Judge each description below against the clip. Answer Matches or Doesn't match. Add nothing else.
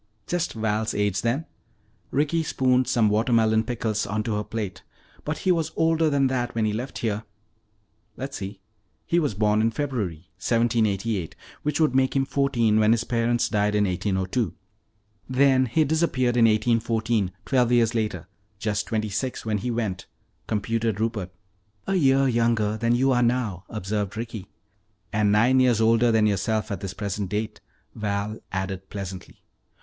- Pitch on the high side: Doesn't match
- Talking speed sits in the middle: Matches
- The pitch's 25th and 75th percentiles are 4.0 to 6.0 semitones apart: Doesn't match